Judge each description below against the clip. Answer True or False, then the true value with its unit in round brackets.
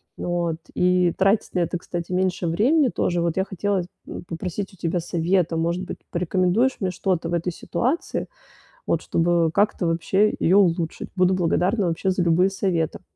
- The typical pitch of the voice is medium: True (180 Hz)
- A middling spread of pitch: False (2.1 semitones)